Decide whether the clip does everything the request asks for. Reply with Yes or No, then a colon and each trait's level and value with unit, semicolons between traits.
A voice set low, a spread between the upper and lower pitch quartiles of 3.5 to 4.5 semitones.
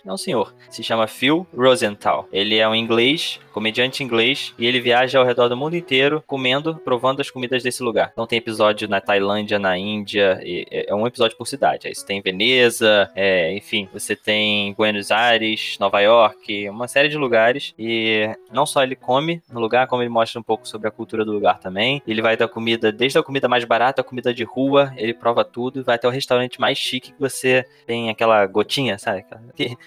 No: low, 120 Hz; average, 3.0 semitones